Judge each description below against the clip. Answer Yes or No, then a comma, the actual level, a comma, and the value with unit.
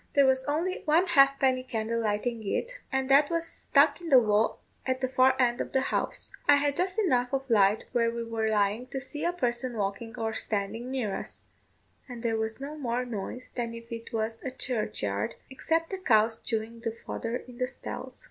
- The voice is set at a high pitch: Yes, high, 245 Hz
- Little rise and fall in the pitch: No, average, 3.4 semitones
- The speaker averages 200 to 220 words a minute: Yes, fast, 205 wpm